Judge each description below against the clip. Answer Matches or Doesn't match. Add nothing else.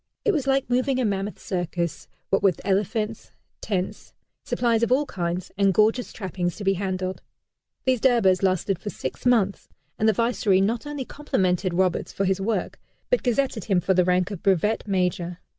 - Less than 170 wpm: Doesn't match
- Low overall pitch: Doesn't match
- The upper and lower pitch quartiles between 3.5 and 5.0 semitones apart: Matches